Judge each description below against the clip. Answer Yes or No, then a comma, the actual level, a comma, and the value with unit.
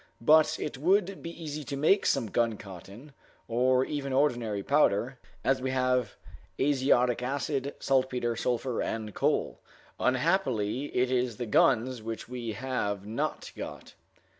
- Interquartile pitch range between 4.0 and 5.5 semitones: No, average, 3.3 semitones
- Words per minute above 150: No, slow, 135 wpm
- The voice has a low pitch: Yes, low, 130 Hz